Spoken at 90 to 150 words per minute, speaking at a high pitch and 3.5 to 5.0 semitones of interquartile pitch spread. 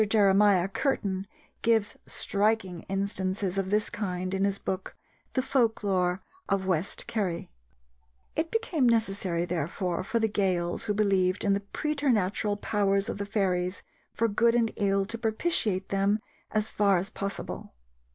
No: average, 145 wpm; high, 200 Hz; narrow, 2.6 semitones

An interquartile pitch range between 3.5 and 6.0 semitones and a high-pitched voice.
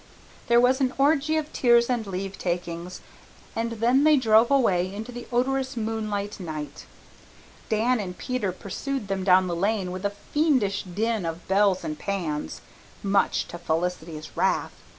Yes: average, 5.2 semitones; high, 205 Hz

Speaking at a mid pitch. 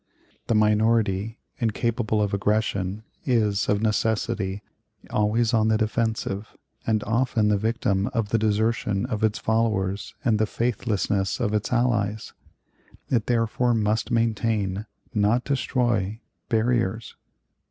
No: low, 110 Hz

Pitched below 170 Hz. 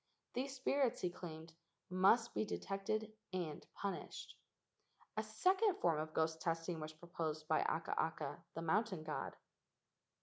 No: medium, 175 Hz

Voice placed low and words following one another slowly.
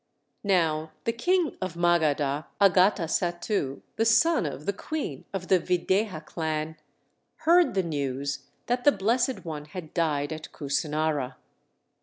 No: medium, 170 Hz; slow, 130 wpm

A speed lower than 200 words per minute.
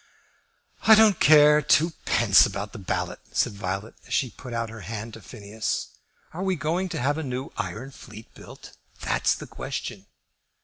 Yes: average, 170 wpm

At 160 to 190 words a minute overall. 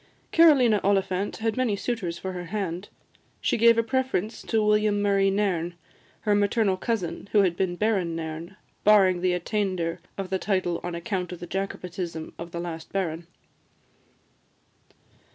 No: average, 150 wpm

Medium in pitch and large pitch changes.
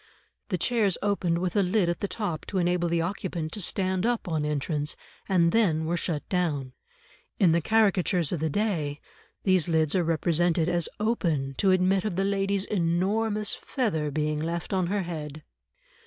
No: medium, 175 Hz; average, 3.6 semitones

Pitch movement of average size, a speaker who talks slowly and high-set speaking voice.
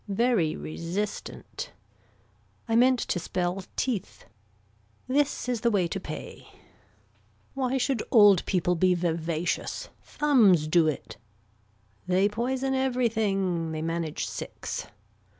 No: wide, 6.4 semitones; slow, 110 wpm; high, 195 Hz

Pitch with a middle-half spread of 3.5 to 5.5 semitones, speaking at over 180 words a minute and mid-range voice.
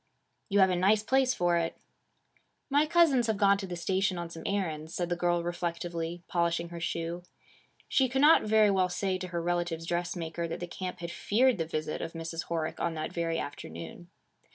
No: average, 2.9 semitones; average, 200 wpm; medium, 175 Hz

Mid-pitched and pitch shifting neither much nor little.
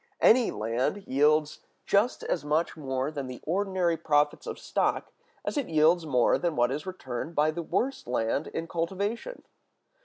Yes: medium, 155 Hz; average, 4.8 semitones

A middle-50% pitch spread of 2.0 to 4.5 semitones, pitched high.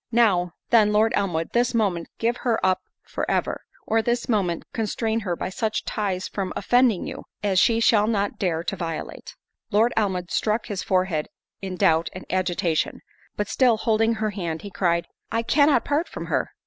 Yes: average, 3.8 semitones; high, 205 Hz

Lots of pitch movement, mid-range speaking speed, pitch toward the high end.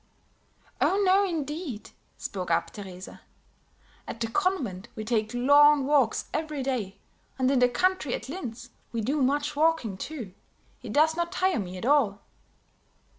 Yes: wide, 5.8 semitones; average, 150 wpm; very high, 265 Hz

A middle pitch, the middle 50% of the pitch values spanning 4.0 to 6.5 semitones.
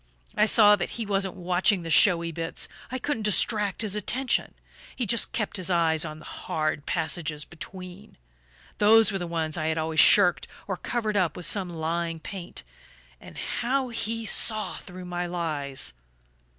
Yes: medium, 180 Hz; average, 4.4 semitones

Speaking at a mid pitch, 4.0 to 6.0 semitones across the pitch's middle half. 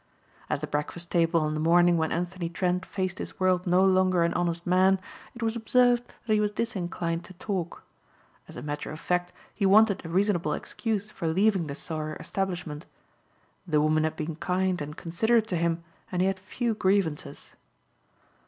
No: medium, 180 Hz; average, 2.7 semitones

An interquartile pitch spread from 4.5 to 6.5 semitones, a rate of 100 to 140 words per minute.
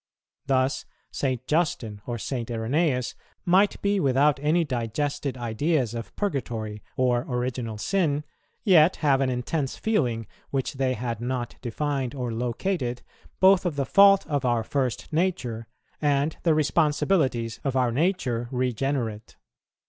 No: average, 4.1 semitones; slow, 135 wpm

